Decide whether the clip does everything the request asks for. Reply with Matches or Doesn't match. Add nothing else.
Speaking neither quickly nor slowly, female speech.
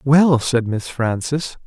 Doesn't match